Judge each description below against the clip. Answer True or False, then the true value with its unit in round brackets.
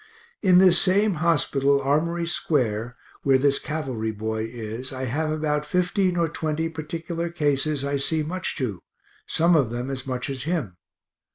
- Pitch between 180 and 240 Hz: False (150 Hz)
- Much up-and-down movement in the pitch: False (4.3 semitones)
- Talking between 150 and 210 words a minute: True (160 wpm)